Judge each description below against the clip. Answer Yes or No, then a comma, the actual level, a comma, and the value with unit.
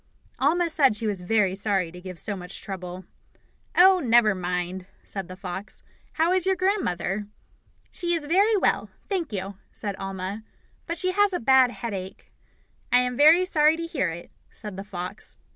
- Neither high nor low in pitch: No, high, 215 Hz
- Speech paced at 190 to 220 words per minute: No, average, 175 wpm